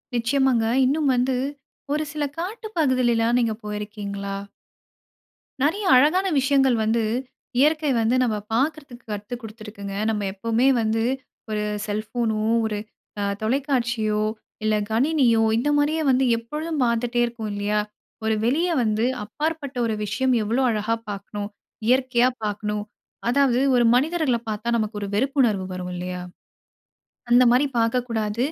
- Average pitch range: Yes, average, 3.9 semitones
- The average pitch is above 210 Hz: Yes, high, 235 Hz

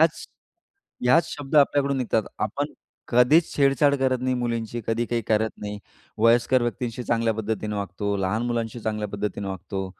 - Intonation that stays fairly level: No, average, 3.3 semitones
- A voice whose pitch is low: Yes, low, 115 Hz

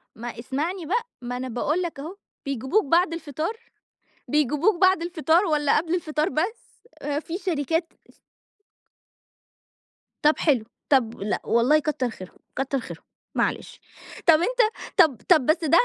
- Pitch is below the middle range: No, very high, 310 Hz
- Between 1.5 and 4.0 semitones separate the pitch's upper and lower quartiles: No, average, 4.4 semitones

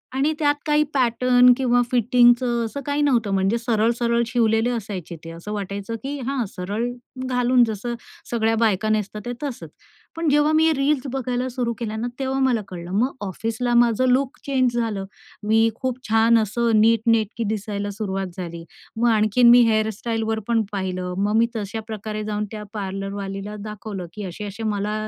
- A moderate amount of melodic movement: Yes, average, 3.0 semitones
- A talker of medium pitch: No, high, 225 Hz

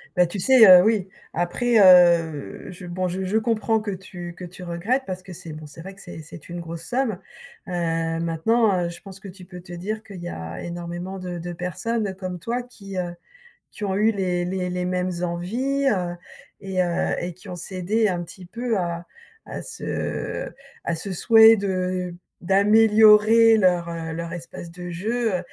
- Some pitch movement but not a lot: Yes, average, 3.3 semitones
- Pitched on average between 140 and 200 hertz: Yes, medium, 185 Hz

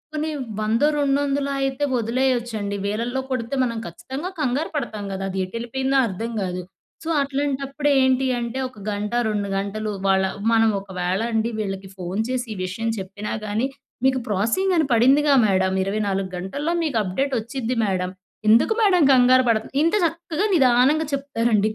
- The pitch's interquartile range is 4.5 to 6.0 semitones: Yes, average, 5.2 semitones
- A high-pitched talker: Yes, high, 235 Hz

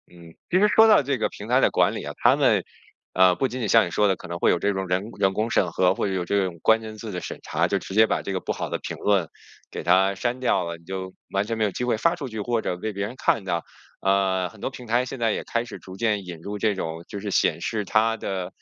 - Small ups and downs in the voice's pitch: No, average, 3.5 semitones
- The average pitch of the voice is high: No, low, 100 Hz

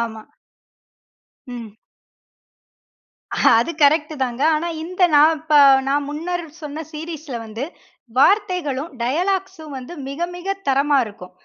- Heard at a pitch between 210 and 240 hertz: No, very high, 300 Hz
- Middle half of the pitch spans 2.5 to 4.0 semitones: No, average, 4.8 semitones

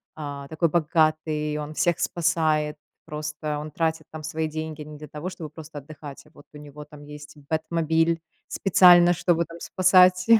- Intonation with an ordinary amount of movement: No, narrow, 1.8 semitones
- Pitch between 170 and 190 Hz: No, medium, 155 Hz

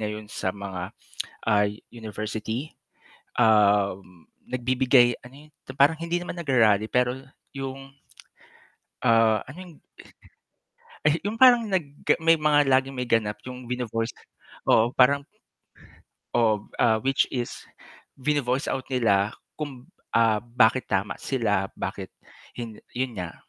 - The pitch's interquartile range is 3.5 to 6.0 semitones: Yes, average, 4.0 semitones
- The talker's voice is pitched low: Yes, low, 120 Hz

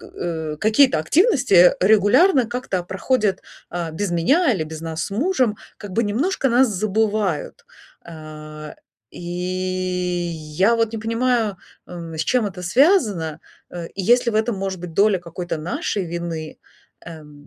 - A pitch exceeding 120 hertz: Yes, medium, 185 Hz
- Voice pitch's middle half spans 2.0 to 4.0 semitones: No, average, 5.3 semitones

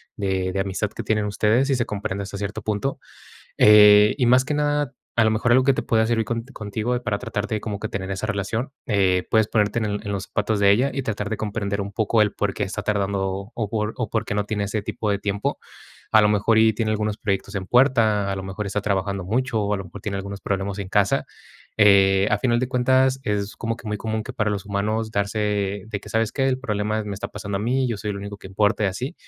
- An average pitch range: No, narrow, 2.0 semitones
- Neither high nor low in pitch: No, low, 105 Hz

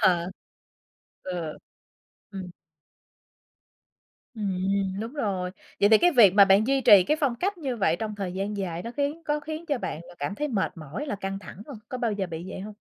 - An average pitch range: No, wide, 5.7 semitones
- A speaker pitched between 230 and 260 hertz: No, high, 205 Hz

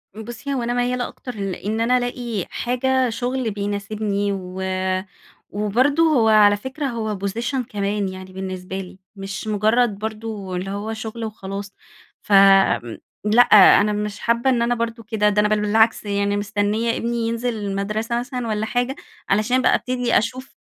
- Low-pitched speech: No, high, 215 Hz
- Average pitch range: Yes, average, 3.0 semitones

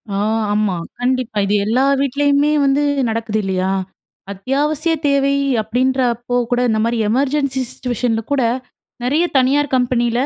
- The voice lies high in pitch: Yes, very high, 255 Hz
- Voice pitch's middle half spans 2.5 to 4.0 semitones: Yes, average, 3.5 semitones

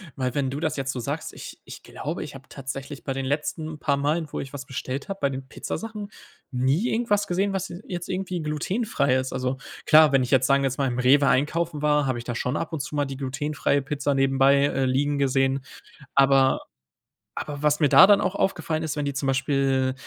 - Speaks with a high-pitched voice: No, medium, 140 Hz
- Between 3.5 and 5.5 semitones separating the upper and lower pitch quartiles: No, average, 2.7 semitones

